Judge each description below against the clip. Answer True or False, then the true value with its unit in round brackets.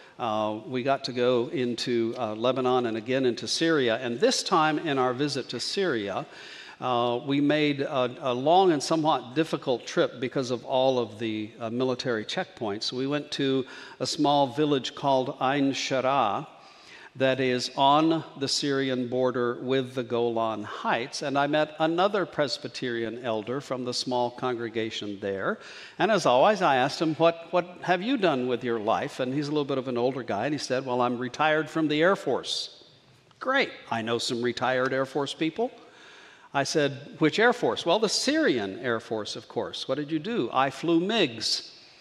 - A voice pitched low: True (130 Hz)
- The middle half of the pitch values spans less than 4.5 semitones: True (3.6 semitones)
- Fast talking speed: False (185 wpm)